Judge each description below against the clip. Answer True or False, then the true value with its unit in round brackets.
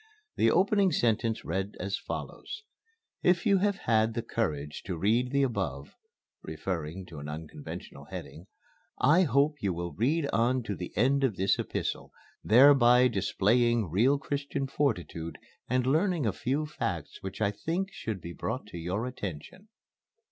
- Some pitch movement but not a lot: False (6.7 semitones)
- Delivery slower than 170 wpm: True (155 wpm)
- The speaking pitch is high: False (115 Hz)